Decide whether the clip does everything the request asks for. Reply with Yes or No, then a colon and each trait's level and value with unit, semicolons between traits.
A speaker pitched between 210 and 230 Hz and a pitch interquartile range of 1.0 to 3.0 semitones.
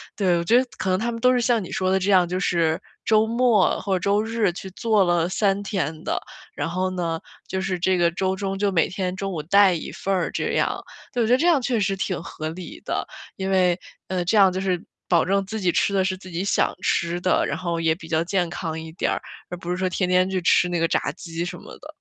No: medium, 185 Hz; narrow, 2.4 semitones